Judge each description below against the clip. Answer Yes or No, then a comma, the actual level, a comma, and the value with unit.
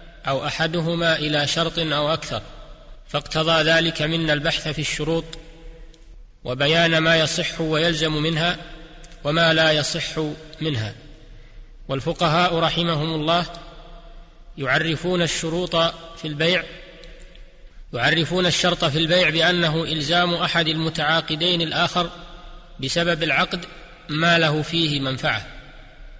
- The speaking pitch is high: No, medium, 165 Hz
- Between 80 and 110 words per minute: Yes, average, 100 wpm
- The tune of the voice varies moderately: No, narrow, 1.6 semitones